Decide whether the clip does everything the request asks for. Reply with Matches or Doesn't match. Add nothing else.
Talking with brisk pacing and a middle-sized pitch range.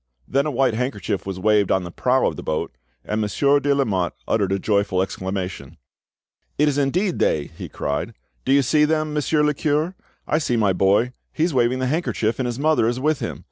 Doesn't match